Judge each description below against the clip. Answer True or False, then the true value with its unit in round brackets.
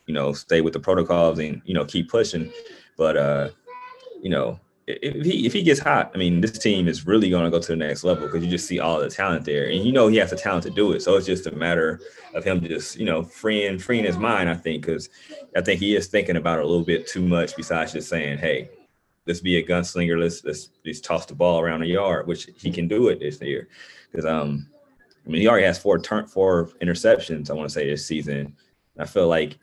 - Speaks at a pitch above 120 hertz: False (85 Hz)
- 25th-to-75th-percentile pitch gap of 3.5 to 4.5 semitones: False (2.6 semitones)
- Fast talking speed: True (255 wpm)